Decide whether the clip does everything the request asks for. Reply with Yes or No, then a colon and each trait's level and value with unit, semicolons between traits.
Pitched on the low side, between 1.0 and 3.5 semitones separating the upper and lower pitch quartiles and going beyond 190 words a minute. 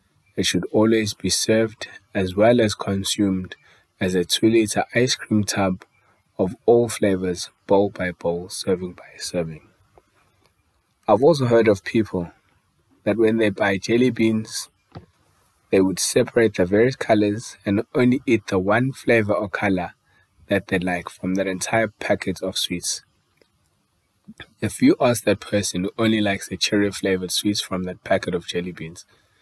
No: low, 105 Hz; average, 3.2 semitones; average, 155 wpm